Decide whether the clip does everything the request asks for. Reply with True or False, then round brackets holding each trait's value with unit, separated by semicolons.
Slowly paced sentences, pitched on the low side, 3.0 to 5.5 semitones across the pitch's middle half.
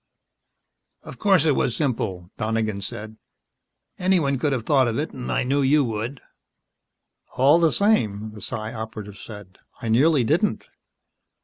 False (145 wpm; 120 Hz; 5.1 semitones)